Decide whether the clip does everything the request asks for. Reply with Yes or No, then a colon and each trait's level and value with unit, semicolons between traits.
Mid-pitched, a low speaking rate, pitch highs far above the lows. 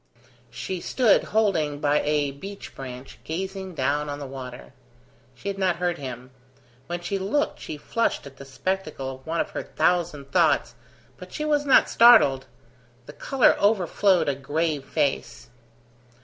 No: medium, 160 Hz; average, 155 wpm; wide, 5.7 semitones